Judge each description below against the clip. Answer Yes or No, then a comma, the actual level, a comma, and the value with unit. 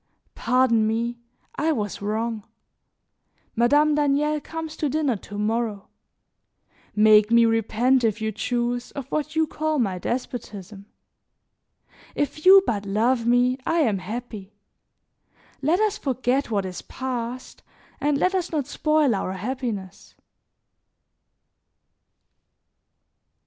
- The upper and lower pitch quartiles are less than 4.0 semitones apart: No, average, 5.2 semitones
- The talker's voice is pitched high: Yes, high, 240 Hz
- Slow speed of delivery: Yes, slow, 115 wpm